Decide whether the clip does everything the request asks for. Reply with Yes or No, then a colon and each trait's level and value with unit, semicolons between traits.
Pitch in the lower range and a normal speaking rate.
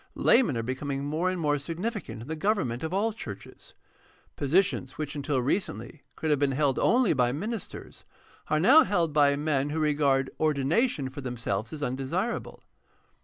No: medium, 150 Hz; average, 170 wpm